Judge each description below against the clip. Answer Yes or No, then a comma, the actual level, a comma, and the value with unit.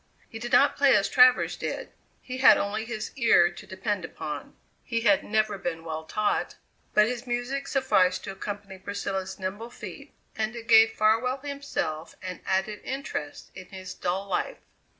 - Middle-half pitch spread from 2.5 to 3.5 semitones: No, average, 4.3 semitones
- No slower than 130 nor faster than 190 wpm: Yes, average, 170 wpm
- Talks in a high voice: Yes, high, 210 Hz